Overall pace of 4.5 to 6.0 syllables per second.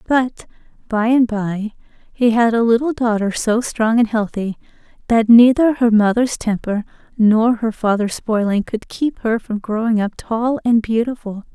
No: 4.3 syllables/s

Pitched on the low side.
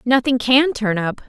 No: high, 245 Hz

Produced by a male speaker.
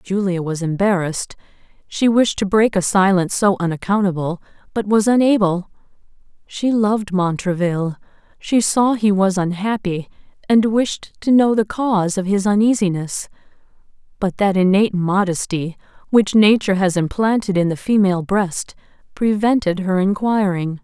No: female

